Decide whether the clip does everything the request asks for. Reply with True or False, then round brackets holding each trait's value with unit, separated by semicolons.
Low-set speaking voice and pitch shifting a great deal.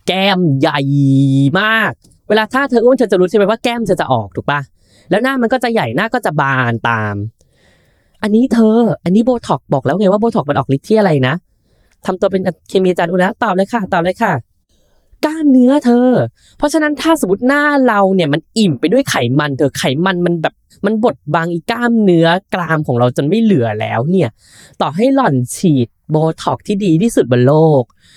False (180 Hz; 8.4 semitones)